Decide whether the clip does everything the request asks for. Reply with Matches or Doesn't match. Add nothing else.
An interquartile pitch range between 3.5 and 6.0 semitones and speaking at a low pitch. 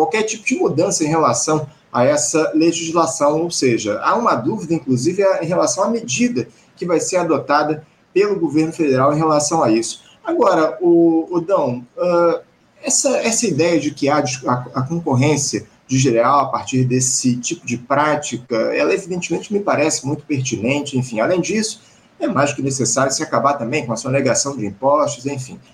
Doesn't match